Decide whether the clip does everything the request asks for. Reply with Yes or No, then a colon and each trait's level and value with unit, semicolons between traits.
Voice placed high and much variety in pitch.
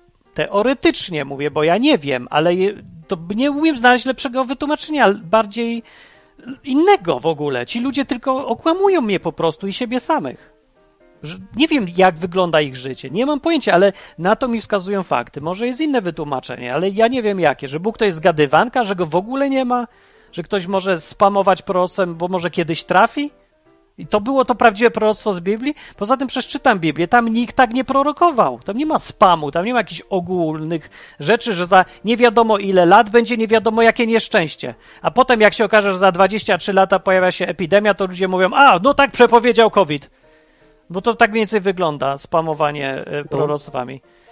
Yes: high, 200 Hz; wide, 6.6 semitones